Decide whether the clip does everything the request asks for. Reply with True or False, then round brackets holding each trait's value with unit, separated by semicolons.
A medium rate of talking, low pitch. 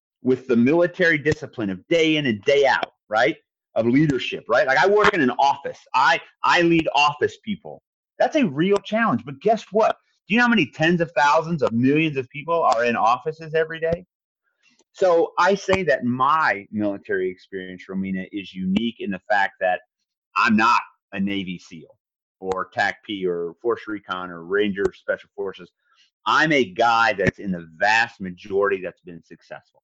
False (180 wpm; 145 Hz)